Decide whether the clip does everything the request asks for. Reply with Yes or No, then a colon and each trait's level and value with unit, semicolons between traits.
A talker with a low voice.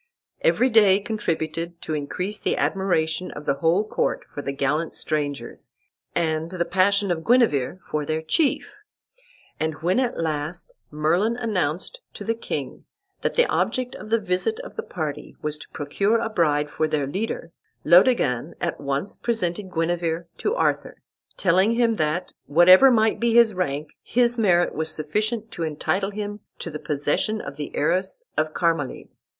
No: medium, 175 Hz